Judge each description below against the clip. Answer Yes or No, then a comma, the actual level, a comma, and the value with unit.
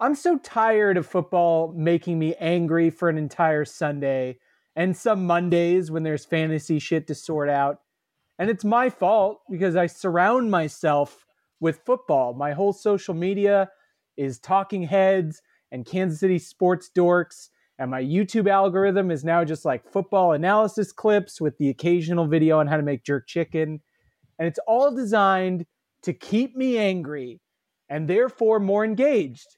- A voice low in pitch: No, medium, 175 Hz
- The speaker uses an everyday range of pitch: Yes, average, 4.0 semitones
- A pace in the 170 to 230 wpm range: No, average, 155 wpm